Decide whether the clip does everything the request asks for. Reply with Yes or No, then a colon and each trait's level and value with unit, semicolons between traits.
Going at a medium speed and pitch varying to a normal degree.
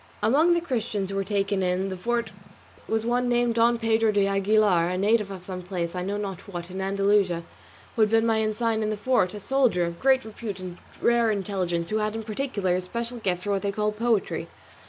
No: fast, 220 wpm; average, 3.2 semitones